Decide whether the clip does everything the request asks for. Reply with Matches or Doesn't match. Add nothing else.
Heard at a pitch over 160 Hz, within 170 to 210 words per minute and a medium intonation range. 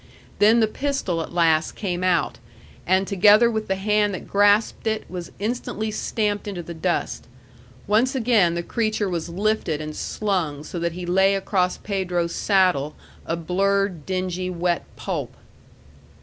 Doesn't match